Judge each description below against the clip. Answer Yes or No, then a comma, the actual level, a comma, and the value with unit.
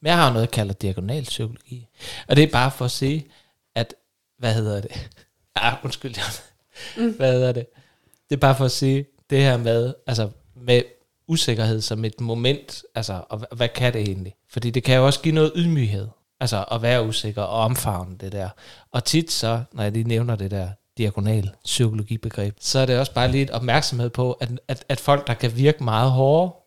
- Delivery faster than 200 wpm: Yes, average, 210 wpm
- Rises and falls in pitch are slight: No, average, 3.5 semitones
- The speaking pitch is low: Yes, low, 120 Hz